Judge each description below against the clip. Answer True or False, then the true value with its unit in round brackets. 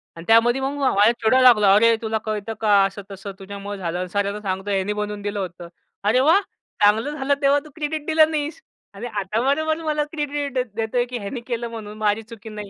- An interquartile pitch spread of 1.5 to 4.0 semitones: False (4.8 semitones)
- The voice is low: False (220 Hz)